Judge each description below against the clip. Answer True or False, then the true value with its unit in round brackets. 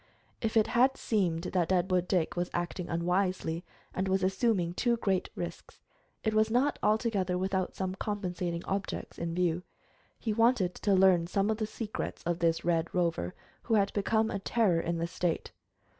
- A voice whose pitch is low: False (185 Hz)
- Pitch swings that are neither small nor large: True (3.6 semitones)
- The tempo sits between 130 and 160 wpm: False (175 wpm)